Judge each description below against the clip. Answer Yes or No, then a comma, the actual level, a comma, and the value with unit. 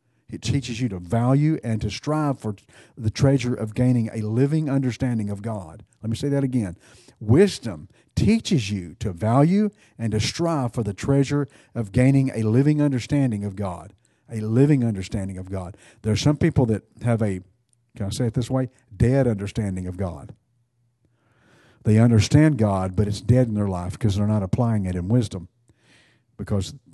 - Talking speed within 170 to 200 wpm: Yes, average, 180 wpm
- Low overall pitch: Yes, low, 115 Hz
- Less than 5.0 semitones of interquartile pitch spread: Yes, average, 3.7 semitones